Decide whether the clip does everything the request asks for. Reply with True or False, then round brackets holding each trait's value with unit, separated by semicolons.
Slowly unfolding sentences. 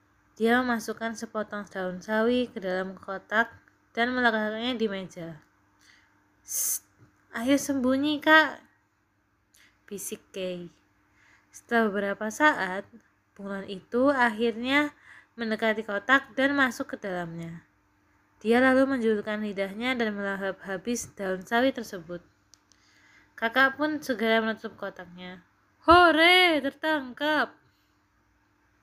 False (95 wpm)